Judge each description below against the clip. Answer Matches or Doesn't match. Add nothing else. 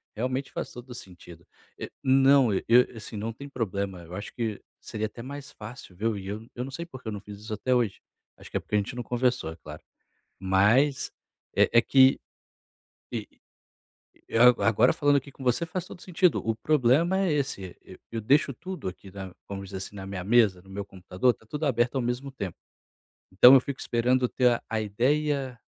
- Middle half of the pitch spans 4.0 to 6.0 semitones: Matches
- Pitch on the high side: Doesn't match